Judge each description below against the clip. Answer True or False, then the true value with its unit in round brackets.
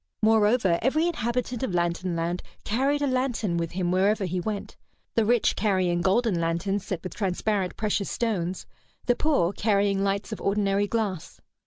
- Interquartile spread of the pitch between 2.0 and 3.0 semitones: False (3.8 semitones)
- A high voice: True (200 Hz)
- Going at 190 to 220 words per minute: False (160 wpm)